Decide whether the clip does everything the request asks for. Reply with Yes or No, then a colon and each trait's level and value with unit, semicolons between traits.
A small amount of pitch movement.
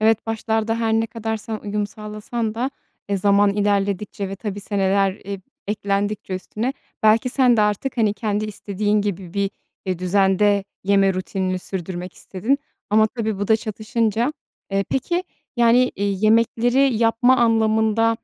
Yes: narrow, 2.2 semitones